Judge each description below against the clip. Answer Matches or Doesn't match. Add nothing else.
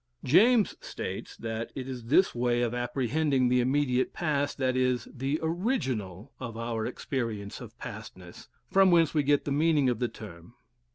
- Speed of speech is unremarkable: Matches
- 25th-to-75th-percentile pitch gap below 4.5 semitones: Matches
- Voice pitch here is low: Matches